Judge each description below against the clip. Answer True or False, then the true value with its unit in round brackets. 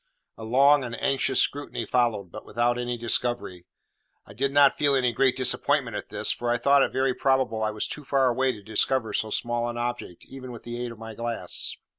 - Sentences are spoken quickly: True (220 wpm)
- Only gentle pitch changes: True (2.3 semitones)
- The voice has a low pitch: True (120 Hz)